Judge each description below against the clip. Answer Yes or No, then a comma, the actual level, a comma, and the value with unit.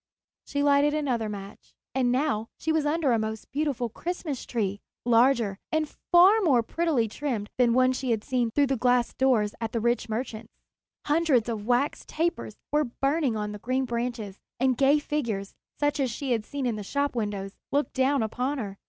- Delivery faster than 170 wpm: Yes, average, 190 wpm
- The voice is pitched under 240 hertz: No, very high, 250 Hz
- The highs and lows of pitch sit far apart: No, average, 4.4 semitones